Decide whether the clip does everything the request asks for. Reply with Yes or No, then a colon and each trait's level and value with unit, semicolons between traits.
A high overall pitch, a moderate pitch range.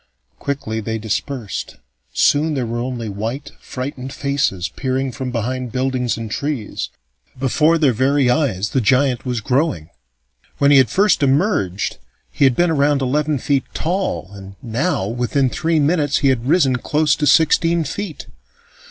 No: low, 135 Hz; average, 3.8 semitones